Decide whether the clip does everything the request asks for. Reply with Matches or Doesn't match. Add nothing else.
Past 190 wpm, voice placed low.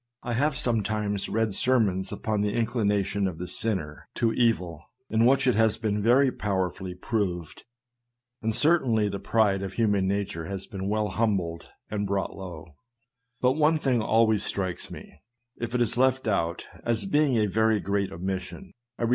Doesn't match